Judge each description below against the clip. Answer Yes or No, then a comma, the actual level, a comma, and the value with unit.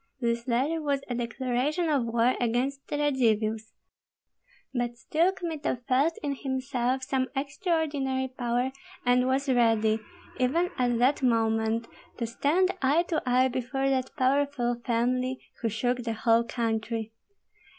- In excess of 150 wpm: No, slow, 135 wpm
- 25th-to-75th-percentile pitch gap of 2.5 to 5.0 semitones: Yes, average, 2.9 semitones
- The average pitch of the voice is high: Yes, very high, 255 Hz